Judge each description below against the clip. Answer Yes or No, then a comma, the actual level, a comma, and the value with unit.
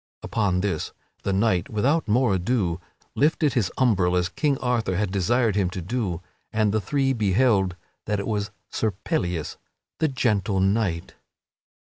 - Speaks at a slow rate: No, average, 150 wpm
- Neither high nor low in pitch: No, low, 105 Hz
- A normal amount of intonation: Yes, average, 4.7 semitones